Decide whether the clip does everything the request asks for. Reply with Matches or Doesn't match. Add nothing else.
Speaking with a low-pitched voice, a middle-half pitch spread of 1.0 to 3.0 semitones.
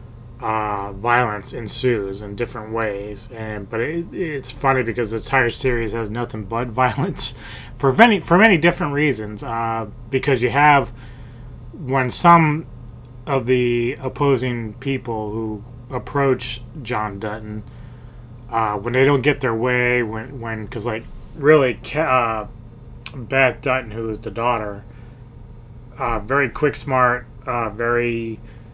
Matches